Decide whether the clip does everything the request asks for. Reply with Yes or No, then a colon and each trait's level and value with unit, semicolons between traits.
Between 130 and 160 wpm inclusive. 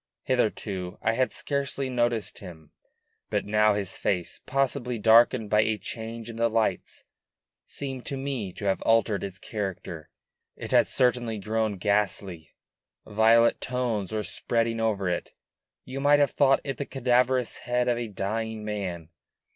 Yes: average, 150 wpm